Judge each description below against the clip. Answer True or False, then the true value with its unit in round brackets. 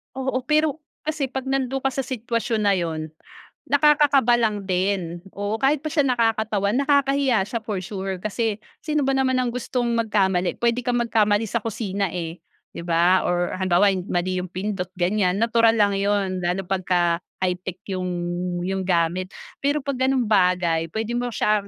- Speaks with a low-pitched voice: False (210 Hz)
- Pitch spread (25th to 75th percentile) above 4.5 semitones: True (5.2 semitones)